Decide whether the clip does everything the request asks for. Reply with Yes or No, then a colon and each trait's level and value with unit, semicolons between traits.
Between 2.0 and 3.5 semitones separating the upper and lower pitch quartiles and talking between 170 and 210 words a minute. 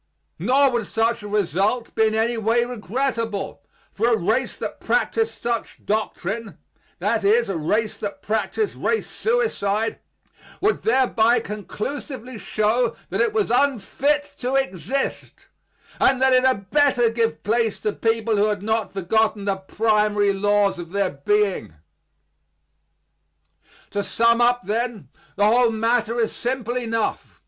No: average, 3.2 semitones; average, 140 wpm